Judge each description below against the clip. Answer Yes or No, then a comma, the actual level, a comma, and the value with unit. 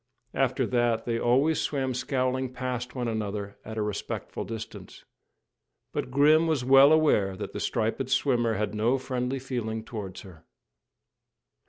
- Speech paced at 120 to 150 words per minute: Yes, average, 145 wpm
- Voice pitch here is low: Yes, low, 125 Hz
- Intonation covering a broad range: No, average, 3.2 semitones